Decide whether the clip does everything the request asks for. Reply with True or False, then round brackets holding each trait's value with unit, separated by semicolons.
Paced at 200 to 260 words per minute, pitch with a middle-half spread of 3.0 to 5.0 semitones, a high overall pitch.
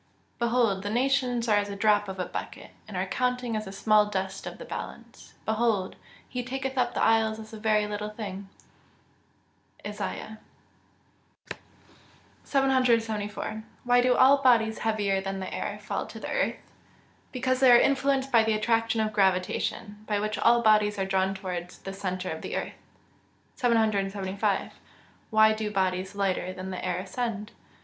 False (165 wpm; 3.4 semitones; 215 Hz)